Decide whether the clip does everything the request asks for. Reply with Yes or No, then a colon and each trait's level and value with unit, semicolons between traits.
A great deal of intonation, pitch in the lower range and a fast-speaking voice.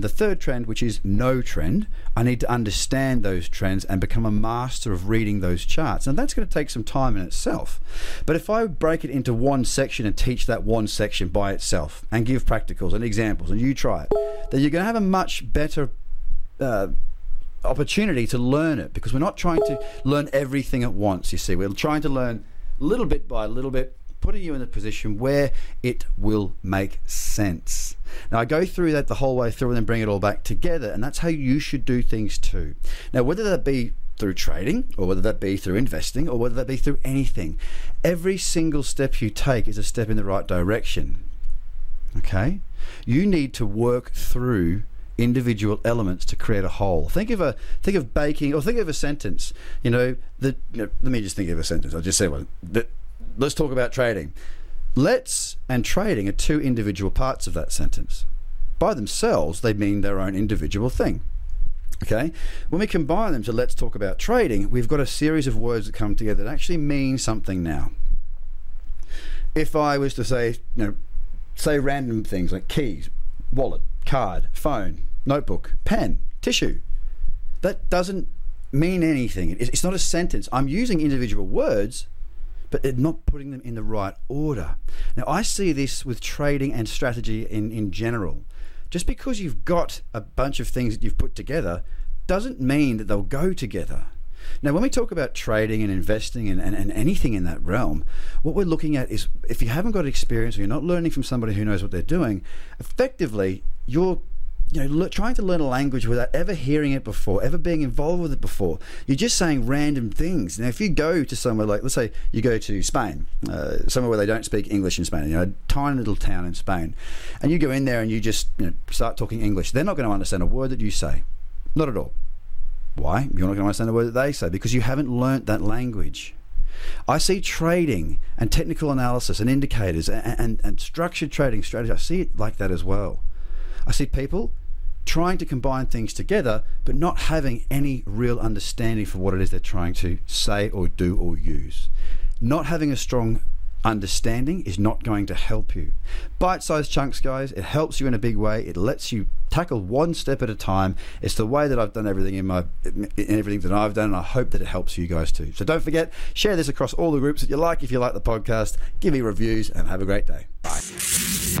Yes: wide, 6.3 semitones; low, 110 Hz; fast, 210 wpm